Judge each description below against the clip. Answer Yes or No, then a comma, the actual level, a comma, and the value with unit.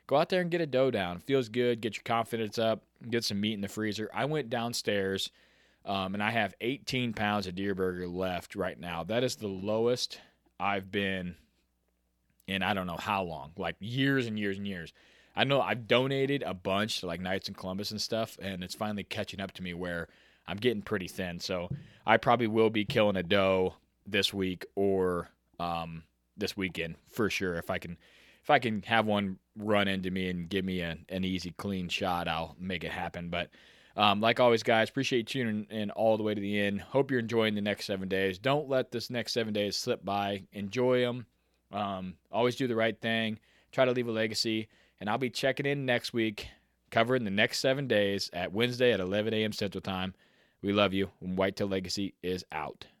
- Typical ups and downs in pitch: Yes, average, 3.5 semitones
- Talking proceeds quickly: Yes, fast, 215 wpm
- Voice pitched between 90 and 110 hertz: Yes, low, 100 Hz